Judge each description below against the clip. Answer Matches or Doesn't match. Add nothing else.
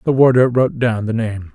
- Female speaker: Doesn't match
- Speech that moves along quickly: Matches